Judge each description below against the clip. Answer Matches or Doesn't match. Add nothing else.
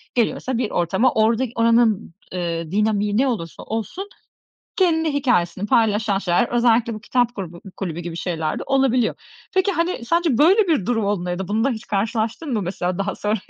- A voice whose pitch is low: Doesn't match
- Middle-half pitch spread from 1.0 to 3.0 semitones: Doesn't match